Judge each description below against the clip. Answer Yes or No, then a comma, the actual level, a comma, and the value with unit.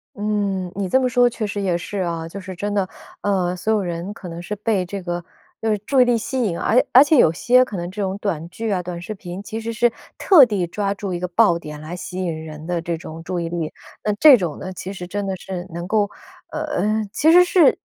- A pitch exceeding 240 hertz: No, high, 195 Hz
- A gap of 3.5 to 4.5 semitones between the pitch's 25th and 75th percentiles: Yes, average, 3.8 semitones